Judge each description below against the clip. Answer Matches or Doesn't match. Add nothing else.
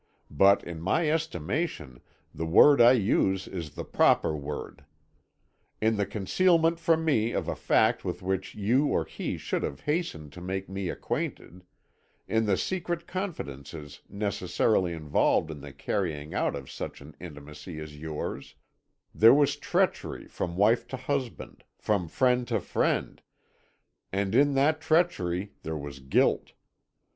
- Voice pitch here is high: Doesn't match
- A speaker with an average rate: Matches